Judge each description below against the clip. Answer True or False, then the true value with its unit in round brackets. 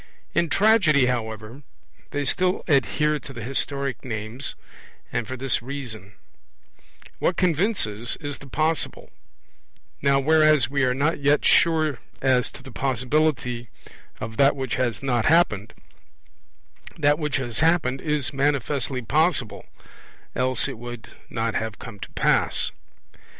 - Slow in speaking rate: True (130 wpm)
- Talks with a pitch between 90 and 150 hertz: True (135 Hz)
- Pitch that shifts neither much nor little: True (4.0 semitones)